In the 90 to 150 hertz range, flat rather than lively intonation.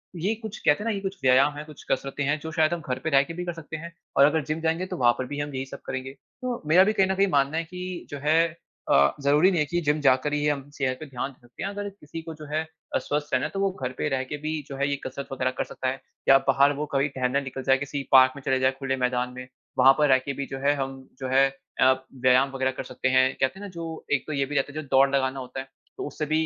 No: medium, 140 Hz; average, 3.2 semitones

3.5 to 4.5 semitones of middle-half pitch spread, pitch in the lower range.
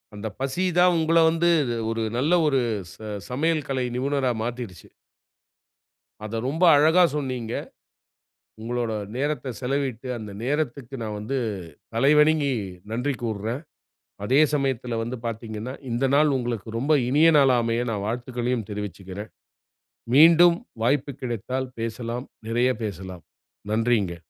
Yes: average, 3.8 semitones; low, 125 Hz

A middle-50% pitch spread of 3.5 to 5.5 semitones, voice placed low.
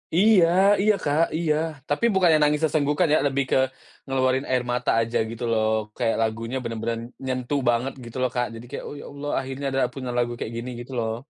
Yes: average, 3.8 semitones; low, 130 Hz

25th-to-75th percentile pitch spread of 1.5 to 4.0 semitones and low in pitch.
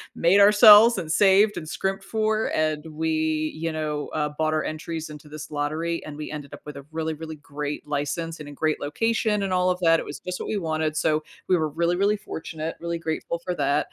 No: average, 3.0 semitones; medium, 160 Hz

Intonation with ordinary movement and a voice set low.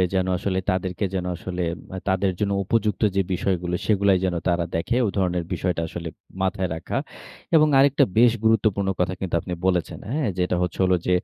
No: narrow, 2.1 semitones; very low, 95 Hz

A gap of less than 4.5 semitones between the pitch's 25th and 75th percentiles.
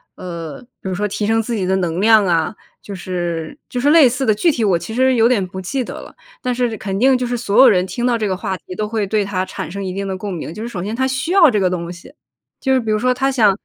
No: average, 4.8 semitones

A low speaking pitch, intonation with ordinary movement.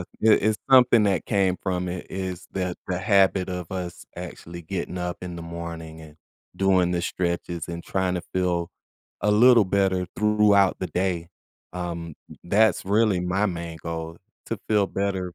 No: very low, 90 Hz; narrow, 2.3 semitones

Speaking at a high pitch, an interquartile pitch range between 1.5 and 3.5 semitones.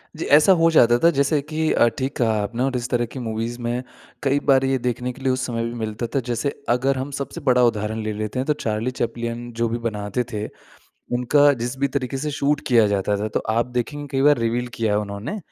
No: low, 125 Hz; average, 3.0 semitones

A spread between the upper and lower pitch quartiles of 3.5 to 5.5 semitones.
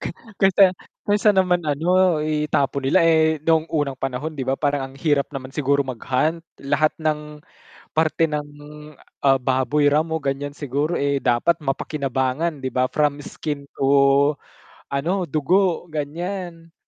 No: average, 2.9 semitones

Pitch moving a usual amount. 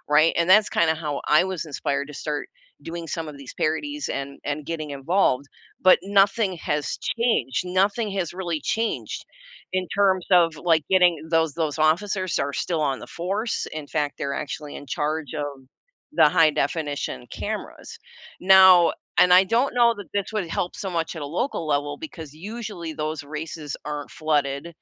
Yes: average, 4.1 semitones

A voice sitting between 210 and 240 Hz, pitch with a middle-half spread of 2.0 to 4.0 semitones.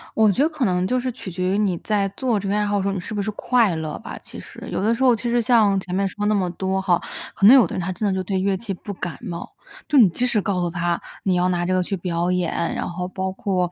No: high, 195 Hz; average, 2.9 semitones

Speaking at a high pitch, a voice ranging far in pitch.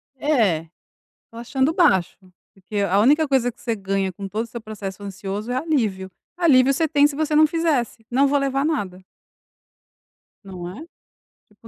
Yes: high, 235 Hz; wide, 6.5 semitones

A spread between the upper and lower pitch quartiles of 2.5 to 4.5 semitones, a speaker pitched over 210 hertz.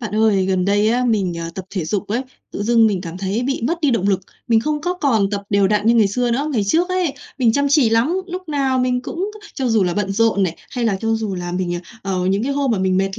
No: average, 5.1 semitones; high, 220 Hz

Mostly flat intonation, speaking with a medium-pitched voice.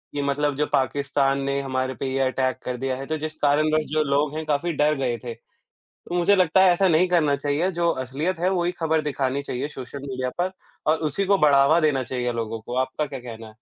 No: average, 3.1 semitones; medium, 145 Hz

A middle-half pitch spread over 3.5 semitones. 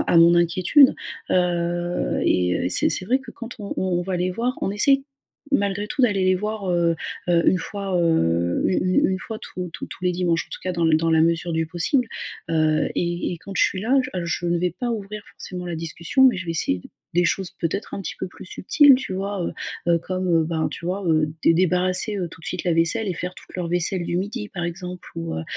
No: average, 2.9 semitones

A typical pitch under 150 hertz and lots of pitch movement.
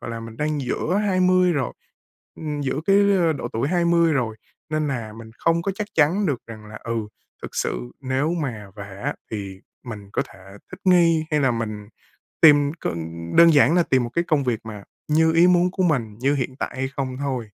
Yes: medium, 140 Hz; wide, 6.5 semitones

